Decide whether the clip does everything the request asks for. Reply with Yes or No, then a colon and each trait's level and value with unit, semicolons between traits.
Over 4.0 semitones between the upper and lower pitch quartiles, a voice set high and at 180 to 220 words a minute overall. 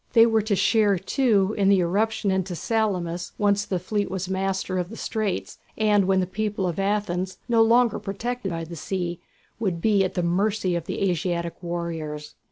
No: average, 3.3 semitones; high, 195 Hz; average, 185 wpm